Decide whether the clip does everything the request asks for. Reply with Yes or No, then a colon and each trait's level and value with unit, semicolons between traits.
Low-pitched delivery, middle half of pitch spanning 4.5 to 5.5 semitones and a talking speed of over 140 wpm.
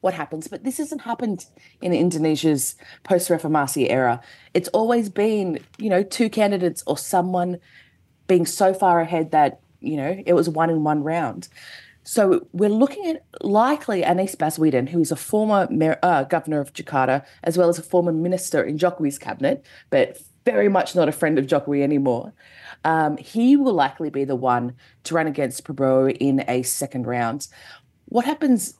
No: medium, 170 Hz; average, 5.2 semitones; average, 175 wpm